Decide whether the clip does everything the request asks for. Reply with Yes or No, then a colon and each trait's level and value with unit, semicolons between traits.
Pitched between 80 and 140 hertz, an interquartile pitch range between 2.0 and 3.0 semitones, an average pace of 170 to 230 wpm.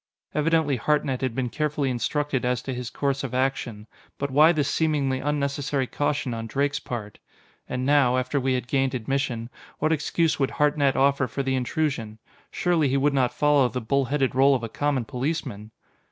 Yes: low, 135 Hz; narrow, 2.5 semitones; average, 180 wpm